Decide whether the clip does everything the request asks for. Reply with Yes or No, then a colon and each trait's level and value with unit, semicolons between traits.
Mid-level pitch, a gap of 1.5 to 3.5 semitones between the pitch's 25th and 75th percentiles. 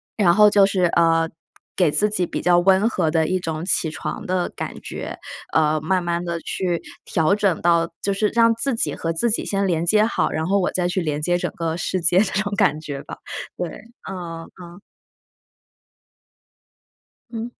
Yes: medium, 180 Hz; average, 3.2 semitones